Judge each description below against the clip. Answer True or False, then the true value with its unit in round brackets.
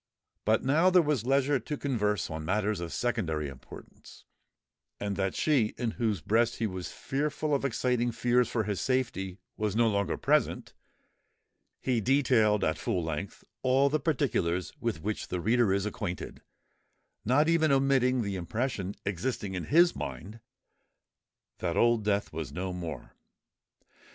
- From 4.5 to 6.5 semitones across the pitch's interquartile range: True (5.4 semitones)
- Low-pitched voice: True (110 Hz)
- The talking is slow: False (150 wpm)